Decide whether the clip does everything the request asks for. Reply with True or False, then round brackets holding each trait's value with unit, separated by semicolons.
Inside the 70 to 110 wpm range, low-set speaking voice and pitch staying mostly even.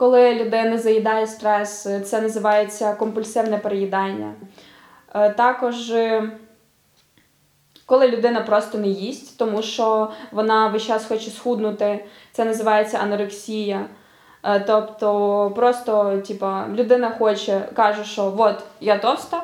False (105 wpm; 220 Hz; 1.6 semitones)